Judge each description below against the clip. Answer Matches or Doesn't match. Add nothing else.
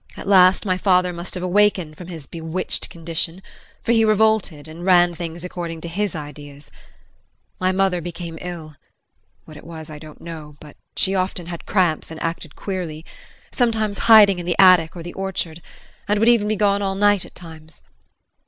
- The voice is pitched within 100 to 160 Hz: Doesn't match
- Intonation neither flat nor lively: Matches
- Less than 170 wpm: Doesn't match